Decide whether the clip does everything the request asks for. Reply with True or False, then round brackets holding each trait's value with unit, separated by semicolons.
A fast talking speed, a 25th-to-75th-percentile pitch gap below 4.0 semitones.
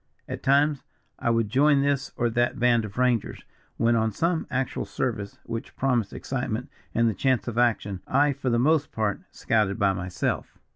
False (180 wpm; 3.3 semitones)